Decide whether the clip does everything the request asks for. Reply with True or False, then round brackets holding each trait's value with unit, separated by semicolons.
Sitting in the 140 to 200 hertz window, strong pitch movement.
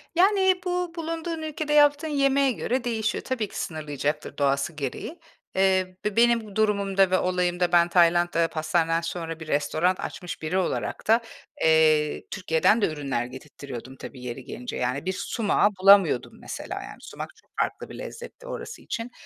True (185 Hz; 7.7 semitones)